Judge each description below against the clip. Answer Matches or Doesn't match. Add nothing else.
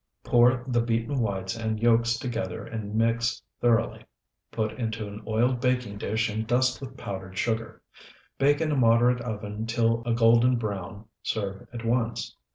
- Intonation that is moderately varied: Doesn't match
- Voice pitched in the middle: Doesn't match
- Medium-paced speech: Matches